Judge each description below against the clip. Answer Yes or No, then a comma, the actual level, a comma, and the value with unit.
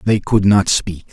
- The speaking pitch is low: Yes, low, 100 Hz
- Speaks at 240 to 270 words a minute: No, fast, 215 wpm